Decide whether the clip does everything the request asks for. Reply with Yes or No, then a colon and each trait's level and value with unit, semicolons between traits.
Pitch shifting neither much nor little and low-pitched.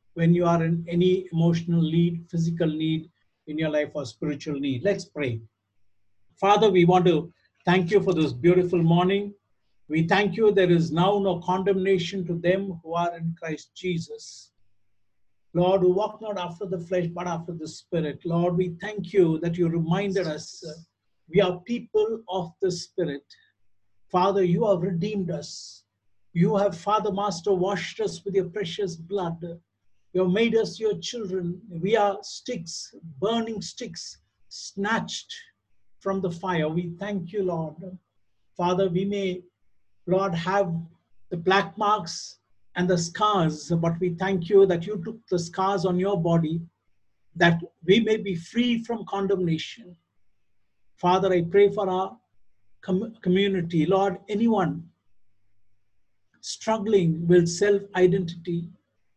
No: average, 3.6 semitones; medium, 180 Hz